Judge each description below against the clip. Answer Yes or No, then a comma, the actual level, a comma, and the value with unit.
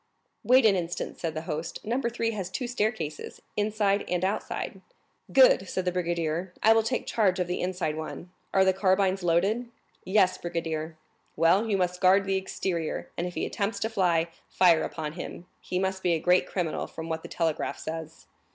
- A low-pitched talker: No, medium, 185 Hz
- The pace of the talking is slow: No, average, 180 wpm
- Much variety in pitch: No, average, 3.3 semitones